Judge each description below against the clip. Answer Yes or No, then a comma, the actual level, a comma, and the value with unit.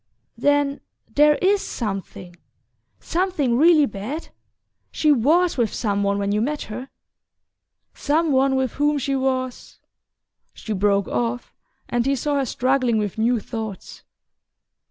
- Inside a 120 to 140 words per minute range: Yes, slow, 135 wpm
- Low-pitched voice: No, very high, 260 Hz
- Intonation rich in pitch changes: No, average, 4.9 semitones